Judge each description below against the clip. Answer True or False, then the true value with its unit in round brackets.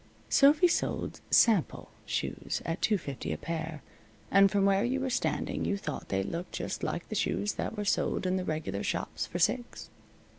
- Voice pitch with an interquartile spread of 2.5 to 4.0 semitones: False (5.6 semitones)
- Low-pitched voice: False (185 Hz)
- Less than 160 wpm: False (185 wpm)